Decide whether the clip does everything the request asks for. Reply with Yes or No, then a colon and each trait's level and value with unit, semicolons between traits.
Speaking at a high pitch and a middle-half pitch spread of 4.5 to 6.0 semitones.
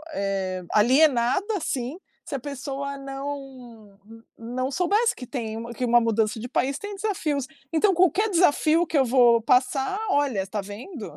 Yes: very high, 265 Hz; average, 4.8 semitones